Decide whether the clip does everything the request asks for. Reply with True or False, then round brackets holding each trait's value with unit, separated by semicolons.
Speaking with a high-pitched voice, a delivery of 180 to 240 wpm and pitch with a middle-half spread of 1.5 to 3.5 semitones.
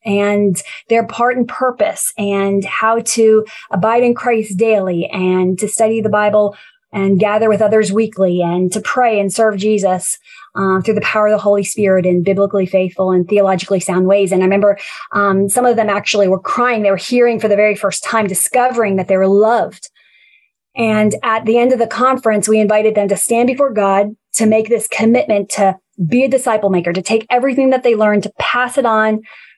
True (215 Hz; 200 wpm; 2.8 semitones)